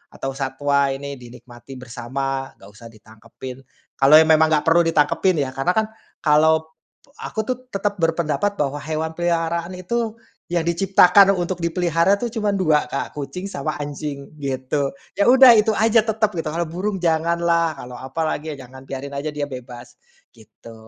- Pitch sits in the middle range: Yes, medium, 155 Hz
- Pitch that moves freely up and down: No, average, 4.6 semitones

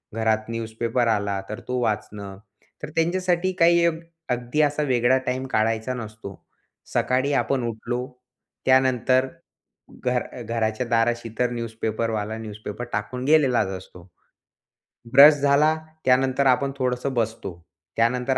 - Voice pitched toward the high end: No, low, 125 Hz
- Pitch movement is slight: No, average, 3.0 semitones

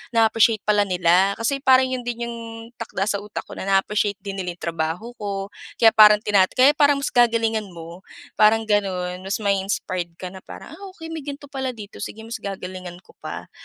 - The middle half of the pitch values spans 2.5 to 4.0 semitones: Yes, average, 3.7 semitones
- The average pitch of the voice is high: Yes, high, 205 Hz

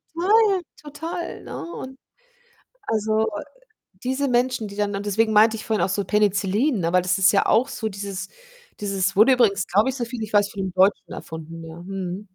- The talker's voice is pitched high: Yes, high, 210 Hz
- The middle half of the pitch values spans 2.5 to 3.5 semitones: No, average, 4.0 semitones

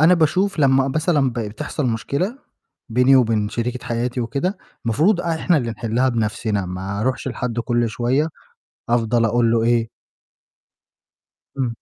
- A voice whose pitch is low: Yes, low, 120 Hz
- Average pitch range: Yes, average, 3.7 semitones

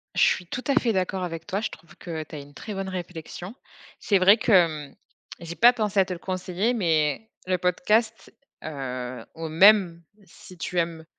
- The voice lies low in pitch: No, medium, 180 Hz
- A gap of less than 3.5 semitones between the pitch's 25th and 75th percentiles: No, average, 3.8 semitones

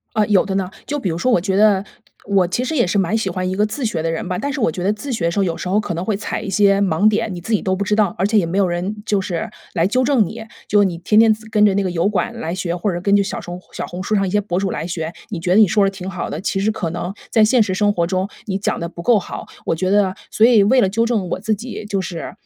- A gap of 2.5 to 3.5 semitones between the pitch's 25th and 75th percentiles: Yes, average, 2.9 semitones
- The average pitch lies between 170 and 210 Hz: Yes, high, 195 Hz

